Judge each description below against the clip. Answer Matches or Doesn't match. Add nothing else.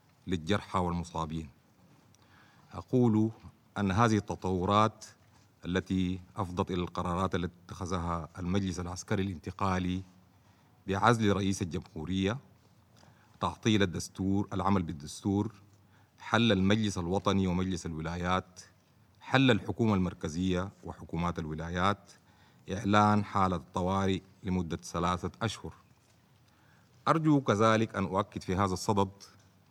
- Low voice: Matches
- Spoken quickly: Doesn't match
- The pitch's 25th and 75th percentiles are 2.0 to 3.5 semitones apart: Matches